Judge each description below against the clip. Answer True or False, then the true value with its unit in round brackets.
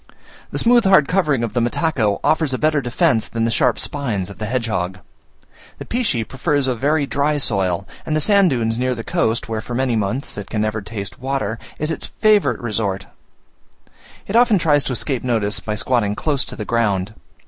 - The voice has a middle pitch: False (120 Hz)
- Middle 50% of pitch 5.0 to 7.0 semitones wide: True (5.3 semitones)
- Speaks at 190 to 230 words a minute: True (195 wpm)